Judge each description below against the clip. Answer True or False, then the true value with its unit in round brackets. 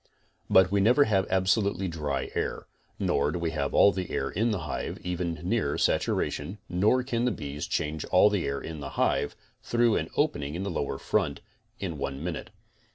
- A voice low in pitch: True (90 Hz)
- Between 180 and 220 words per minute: True (195 wpm)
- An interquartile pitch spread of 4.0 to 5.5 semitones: True (5.2 semitones)